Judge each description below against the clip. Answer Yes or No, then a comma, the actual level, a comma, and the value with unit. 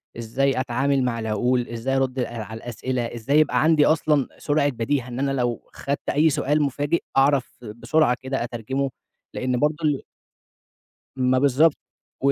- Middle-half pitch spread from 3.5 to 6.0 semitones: No, average, 2.9 semitones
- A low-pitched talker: Yes, low, 130 Hz